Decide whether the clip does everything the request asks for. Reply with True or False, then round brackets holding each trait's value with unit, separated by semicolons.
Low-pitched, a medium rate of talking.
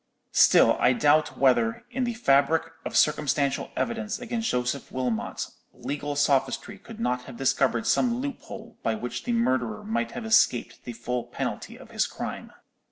False (145 Hz; 160 wpm)